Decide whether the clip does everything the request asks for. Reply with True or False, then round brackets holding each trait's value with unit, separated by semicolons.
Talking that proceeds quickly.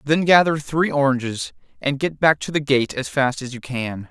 True (220 wpm)